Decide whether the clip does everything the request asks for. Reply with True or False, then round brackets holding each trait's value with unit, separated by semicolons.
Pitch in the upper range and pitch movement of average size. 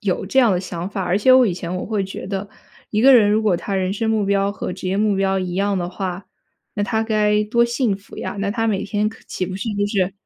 False (200 Hz; 2.2 semitones)